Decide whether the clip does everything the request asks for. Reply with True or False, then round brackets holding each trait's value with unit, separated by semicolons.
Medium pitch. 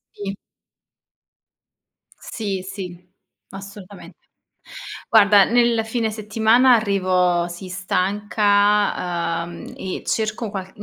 False (200 Hz)